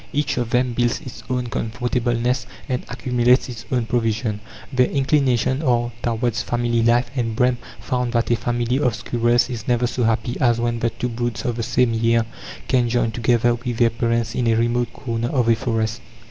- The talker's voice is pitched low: Yes, low, 120 Hz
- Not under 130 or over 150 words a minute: No, average, 195 wpm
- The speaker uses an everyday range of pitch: No, narrow, 1.2 semitones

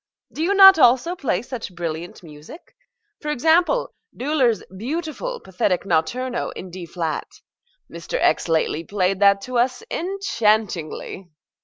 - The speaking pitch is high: Yes, high, 235 Hz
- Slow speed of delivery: Yes, slow, 130 wpm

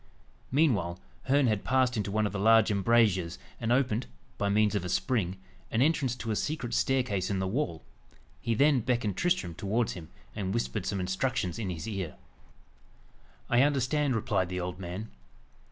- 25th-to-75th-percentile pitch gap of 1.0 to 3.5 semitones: No, average, 5.0 semitones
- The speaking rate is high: No, average, 170 wpm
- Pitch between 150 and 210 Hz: No, low, 110 Hz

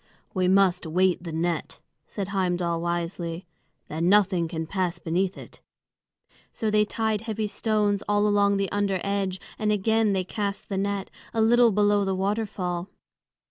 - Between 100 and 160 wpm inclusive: Yes, average, 155 wpm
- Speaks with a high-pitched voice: Yes, high, 195 Hz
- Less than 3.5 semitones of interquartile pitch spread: Yes, average, 2.7 semitones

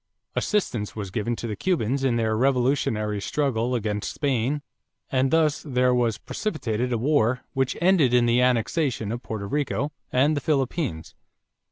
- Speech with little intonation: No, average, 4.3 semitones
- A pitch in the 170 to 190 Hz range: No, low, 125 Hz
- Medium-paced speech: Yes, average, 155 wpm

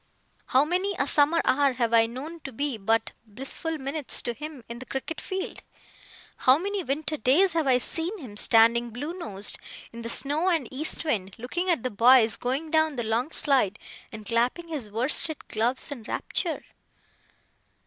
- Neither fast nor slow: Yes, average, 175 wpm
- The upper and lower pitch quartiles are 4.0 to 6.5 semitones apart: Yes, average, 5.3 semitones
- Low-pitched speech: No, very high, 270 Hz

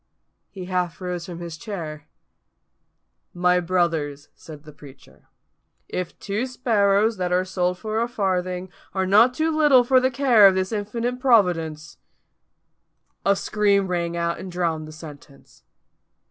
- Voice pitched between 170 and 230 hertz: Yes, medium, 185 Hz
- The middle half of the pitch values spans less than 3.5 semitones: No, average, 4.1 semitones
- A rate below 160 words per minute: Yes, average, 145 wpm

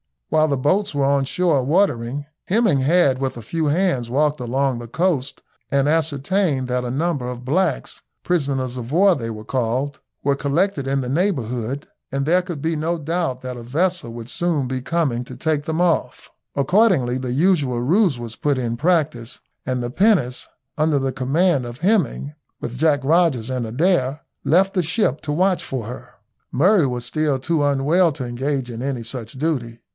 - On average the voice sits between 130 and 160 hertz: Yes, medium, 140 Hz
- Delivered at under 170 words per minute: No, average, 180 wpm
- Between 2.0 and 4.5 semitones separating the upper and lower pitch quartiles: No, average, 4.9 semitones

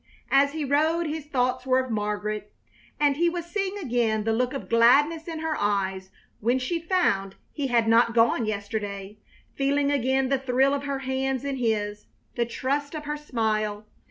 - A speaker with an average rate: Yes, average, 180 wpm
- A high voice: Yes, very high, 260 Hz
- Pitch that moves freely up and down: No, average, 4.7 semitones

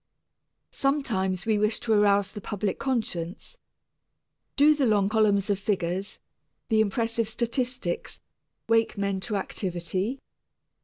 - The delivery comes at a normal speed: No, slow, 115 wpm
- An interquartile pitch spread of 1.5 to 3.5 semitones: Yes, average, 3.0 semitones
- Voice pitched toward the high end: Yes, high, 210 Hz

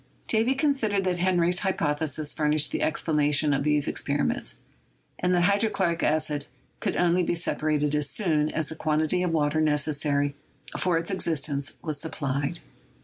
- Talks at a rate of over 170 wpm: No, average, 155 wpm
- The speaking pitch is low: No, medium, 155 Hz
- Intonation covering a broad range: No, average, 3.3 semitones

